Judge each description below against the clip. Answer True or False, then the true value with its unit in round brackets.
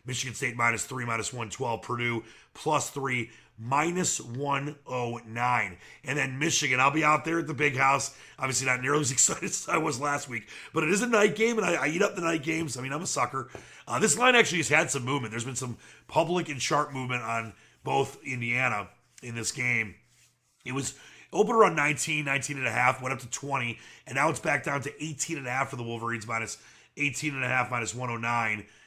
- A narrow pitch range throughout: False (3.8 semitones)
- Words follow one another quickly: True (220 wpm)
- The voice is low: True (130 Hz)